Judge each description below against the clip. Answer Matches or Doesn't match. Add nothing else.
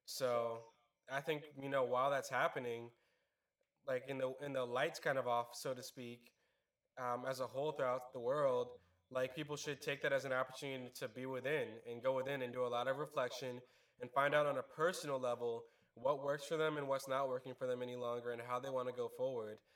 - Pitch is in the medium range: Doesn't match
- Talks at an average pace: Doesn't match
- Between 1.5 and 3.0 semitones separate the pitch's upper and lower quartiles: Matches